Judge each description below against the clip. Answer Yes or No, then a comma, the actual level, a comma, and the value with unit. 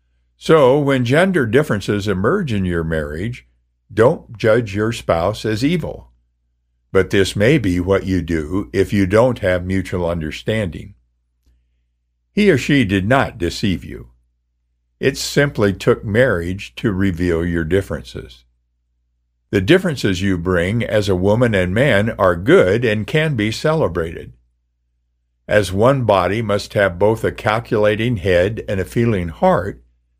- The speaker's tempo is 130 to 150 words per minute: Yes, average, 140 wpm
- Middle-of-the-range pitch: No, very low, 95 Hz